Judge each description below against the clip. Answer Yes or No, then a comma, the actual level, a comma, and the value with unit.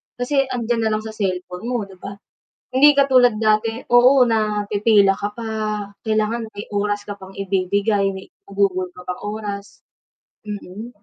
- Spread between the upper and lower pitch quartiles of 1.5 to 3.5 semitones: Yes, average, 2.7 semitones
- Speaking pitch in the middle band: No, high, 210 Hz